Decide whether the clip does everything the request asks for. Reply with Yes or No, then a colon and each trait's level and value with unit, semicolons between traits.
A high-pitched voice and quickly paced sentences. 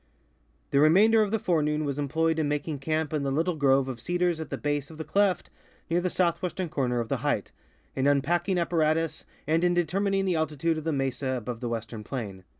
No: medium, 155 Hz; fast, 220 wpm